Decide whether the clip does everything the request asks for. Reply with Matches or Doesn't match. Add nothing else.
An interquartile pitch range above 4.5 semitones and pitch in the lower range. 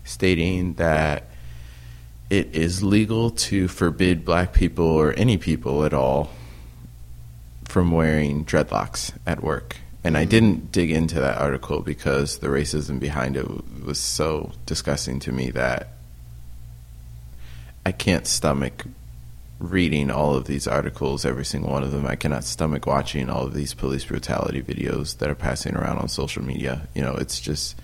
Matches